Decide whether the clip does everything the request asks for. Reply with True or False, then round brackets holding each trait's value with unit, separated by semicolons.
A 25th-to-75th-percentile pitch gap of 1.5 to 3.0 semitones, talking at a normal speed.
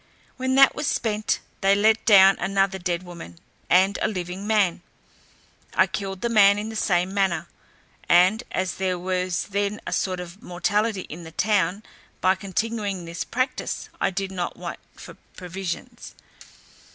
True (2.6 semitones; 150 wpm)